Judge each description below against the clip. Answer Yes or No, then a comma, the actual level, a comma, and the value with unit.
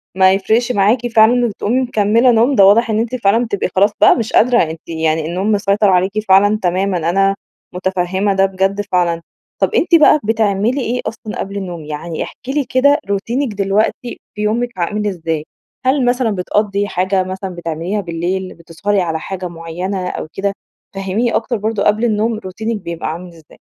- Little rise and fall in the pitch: No, average, 3.6 semitones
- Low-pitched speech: No, high, 200 Hz